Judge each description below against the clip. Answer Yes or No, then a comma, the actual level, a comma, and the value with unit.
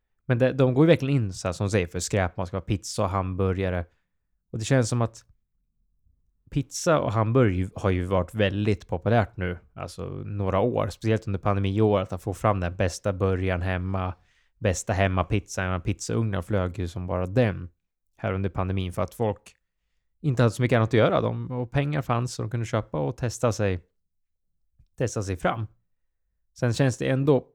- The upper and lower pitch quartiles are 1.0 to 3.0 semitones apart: No, average, 4.3 semitones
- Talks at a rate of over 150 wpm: Yes, average, 190 wpm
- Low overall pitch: Yes, low, 100 Hz